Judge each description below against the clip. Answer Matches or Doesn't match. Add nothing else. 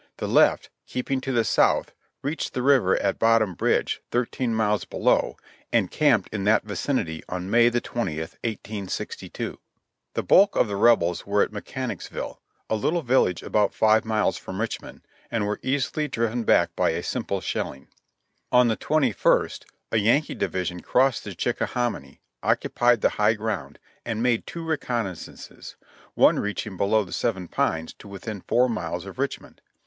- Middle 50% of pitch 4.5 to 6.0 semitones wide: Doesn't match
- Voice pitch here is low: Matches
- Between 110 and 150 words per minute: Doesn't match